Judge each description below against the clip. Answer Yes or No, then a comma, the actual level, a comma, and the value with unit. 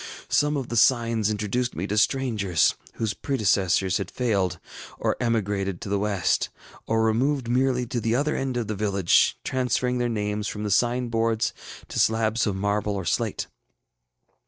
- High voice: No, low, 110 Hz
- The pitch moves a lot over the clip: No, average, 3.3 semitones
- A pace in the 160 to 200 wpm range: Yes, average, 165 wpm